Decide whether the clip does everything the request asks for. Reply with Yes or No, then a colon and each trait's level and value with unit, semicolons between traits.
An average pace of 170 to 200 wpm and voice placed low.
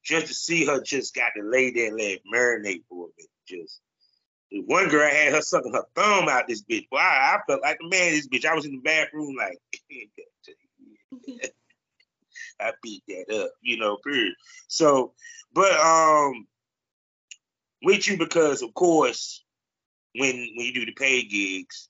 No: average, 180 wpm; medium, 165 Hz